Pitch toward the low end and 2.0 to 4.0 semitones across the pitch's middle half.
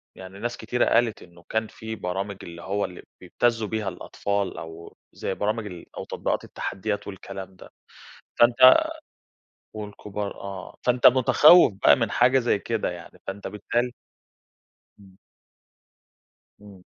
Yes: low, 105 Hz; average, 3.5 semitones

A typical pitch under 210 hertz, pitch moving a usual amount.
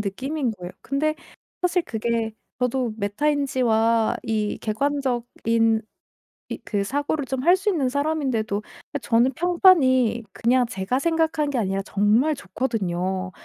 No: very high, 250 Hz; average, 4.8 semitones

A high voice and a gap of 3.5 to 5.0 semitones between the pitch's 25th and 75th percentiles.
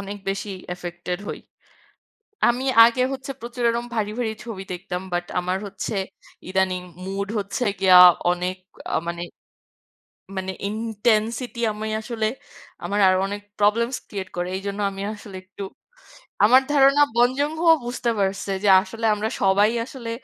Yes: high, 205 Hz; average, 3.8 semitones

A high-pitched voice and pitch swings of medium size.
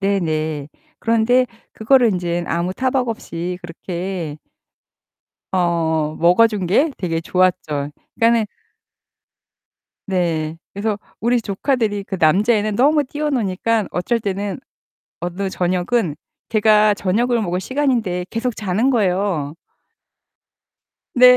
Yes: high, 200 Hz; average, 4.7 semitones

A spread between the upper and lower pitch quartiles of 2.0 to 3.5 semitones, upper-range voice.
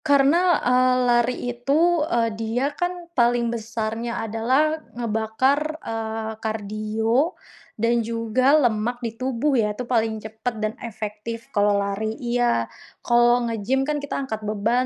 Yes: average, 2.8 semitones; high, 235 Hz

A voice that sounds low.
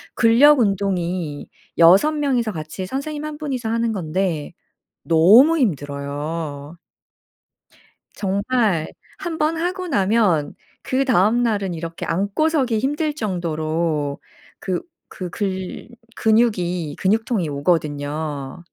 No: high, 195 Hz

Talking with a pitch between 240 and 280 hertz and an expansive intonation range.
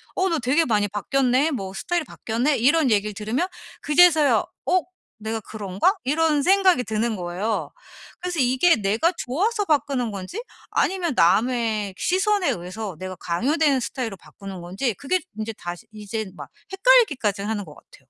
Yes: high, 245 Hz; wide, 7.9 semitones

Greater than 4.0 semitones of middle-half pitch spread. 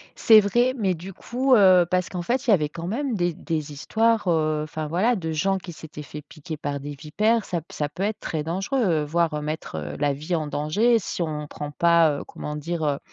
Yes: average, 4.6 semitones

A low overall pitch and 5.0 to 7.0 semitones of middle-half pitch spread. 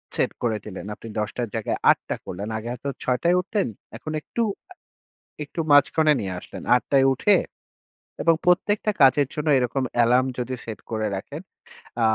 Yes: low, 130 Hz; wide, 5.6 semitones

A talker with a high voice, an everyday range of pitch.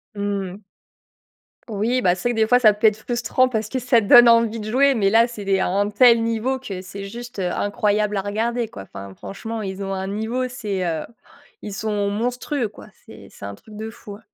Yes: high, 215 Hz; average, 3.0 semitones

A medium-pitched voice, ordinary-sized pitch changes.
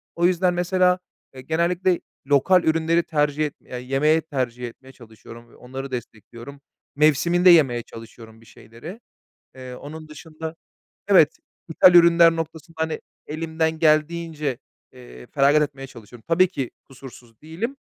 Yes: medium, 155 Hz; average, 4.5 semitones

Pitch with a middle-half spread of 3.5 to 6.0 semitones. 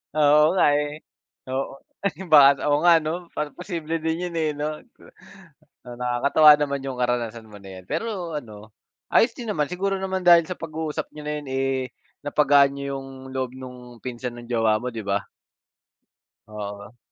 Yes: average, 4.3 semitones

